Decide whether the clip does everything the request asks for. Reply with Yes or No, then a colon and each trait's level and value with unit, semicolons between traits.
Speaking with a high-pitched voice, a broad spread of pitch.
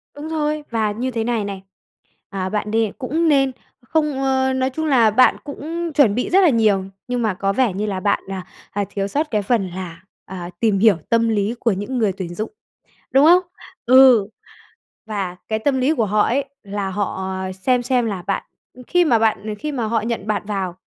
No: high, 225 Hz; average, 4.9 semitones